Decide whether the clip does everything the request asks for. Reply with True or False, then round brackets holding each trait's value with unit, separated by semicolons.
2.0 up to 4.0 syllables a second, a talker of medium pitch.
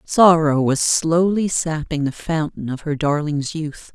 True (3.9 syllables/s; 155 Hz)